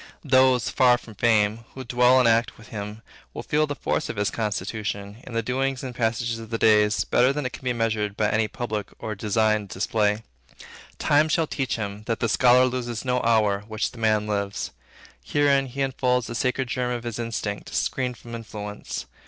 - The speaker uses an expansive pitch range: No, average, 2.9 semitones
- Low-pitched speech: Yes, low, 115 Hz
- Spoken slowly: No, average, 195 wpm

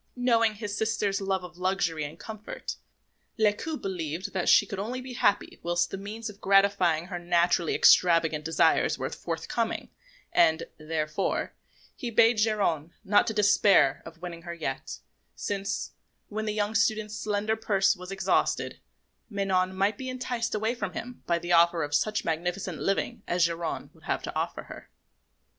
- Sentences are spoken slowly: No, average, 160 wpm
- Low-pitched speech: No, high, 195 Hz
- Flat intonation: No, average, 3.9 semitones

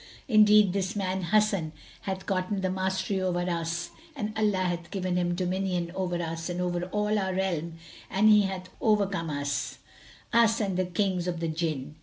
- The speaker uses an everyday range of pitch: No, narrow, 2.3 semitones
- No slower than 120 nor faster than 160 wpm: No, average, 175 wpm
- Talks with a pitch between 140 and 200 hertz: Yes, medium, 185 Hz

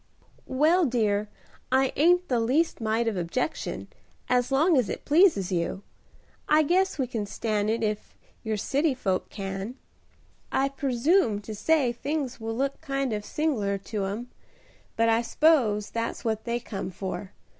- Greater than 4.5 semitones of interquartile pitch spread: Yes, average, 5.1 semitones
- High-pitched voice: Yes, high, 235 Hz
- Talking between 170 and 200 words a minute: No, average, 155 wpm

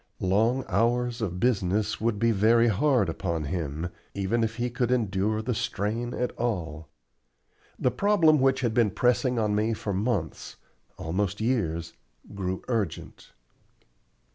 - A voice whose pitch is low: Yes, low, 110 Hz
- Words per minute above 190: No, average, 140 wpm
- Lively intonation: No, average, 4.2 semitones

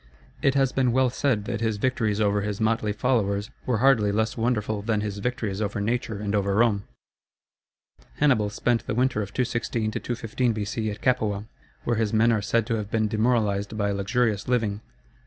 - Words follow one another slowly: No, average, 180 wpm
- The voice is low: Yes, low, 110 Hz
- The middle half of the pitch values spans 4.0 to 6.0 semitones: No, average, 2.7 semitones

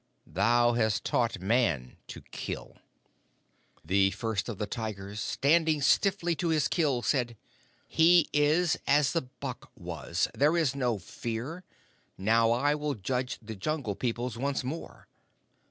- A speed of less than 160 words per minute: Yes, average, 140 wpm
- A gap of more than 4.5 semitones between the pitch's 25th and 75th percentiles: Yes, average, 5.2 semitones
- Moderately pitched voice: No, low, 125 Hz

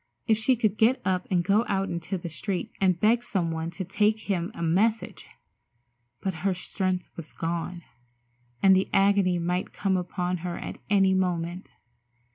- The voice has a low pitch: No, medium, 185 Hz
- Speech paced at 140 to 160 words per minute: No, average, 170 wpm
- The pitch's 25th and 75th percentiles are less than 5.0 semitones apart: Yes, narrow, 2.5 semitones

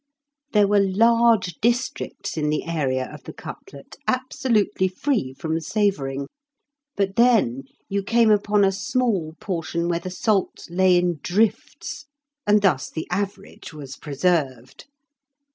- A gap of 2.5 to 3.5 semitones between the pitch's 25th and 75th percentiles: No, average, 5.0 semitones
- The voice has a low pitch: No, high, 190 Hz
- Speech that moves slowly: Yes, slow, 130 wpm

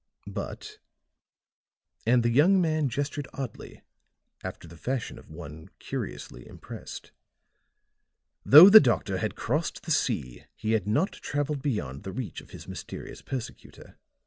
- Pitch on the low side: Yes, low, 125 Hz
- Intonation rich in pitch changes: Yes, wide, 7.1 semitones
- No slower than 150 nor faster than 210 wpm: No, slow, 135 wpm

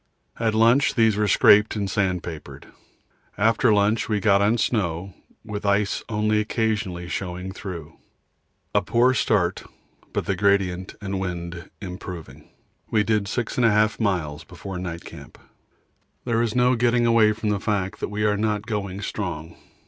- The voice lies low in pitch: Yes, low, 105 Hz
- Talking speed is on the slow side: No, average, 155 wpm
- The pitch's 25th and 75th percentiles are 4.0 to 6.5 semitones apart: No, average, 2.9 semitones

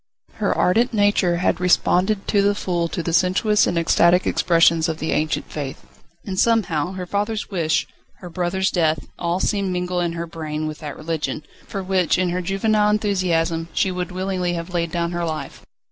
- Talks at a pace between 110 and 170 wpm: No, average, 185 wpm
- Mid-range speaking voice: Yes, medium, 180 Hz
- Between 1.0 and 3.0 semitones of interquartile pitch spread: Yes, narrow, 2.4 semitones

